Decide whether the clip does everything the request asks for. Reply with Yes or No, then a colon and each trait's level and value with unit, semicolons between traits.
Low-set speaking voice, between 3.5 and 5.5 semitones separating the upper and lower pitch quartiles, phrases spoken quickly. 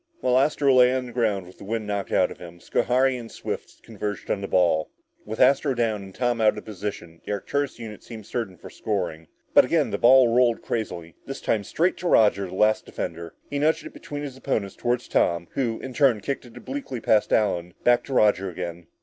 Yes: low, 110 Hz; average, 4.7 semitones; fast, 220 wpm